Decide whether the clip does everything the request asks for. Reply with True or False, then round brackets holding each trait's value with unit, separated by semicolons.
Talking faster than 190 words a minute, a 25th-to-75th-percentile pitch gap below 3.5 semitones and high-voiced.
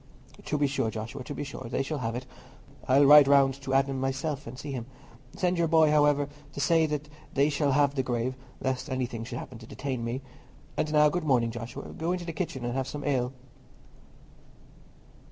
False (200 wpm; 2.7 semitones; 135 Hz)